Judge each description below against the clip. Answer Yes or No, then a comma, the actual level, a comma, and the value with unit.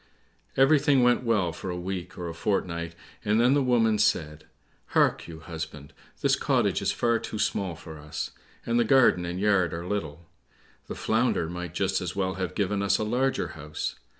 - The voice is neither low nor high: No, very low, 95 Hz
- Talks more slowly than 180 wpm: No, average, 185 wpm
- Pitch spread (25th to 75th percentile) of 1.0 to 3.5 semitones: No, average, 5.3 semitones